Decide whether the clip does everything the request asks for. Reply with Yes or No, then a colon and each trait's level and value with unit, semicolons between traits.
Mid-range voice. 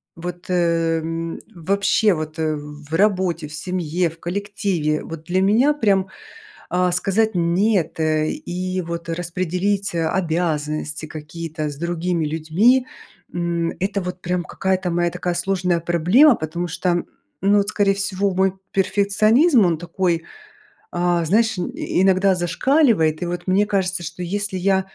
Yes: medium, 180 Hz